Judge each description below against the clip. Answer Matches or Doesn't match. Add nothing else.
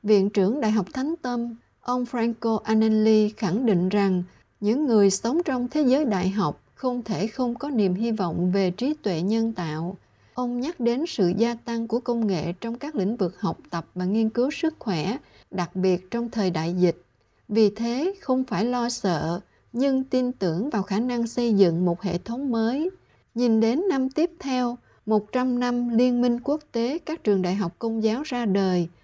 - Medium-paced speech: Matches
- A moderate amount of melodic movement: Matches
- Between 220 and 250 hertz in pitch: Matches